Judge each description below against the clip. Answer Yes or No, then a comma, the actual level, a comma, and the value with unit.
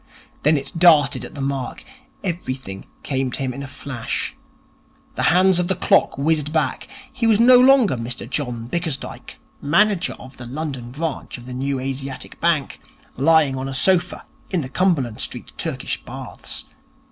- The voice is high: No, medium, 140 Hz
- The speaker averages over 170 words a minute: No, average, 165 wpm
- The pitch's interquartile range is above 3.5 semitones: Yes, average, 4.8 semitones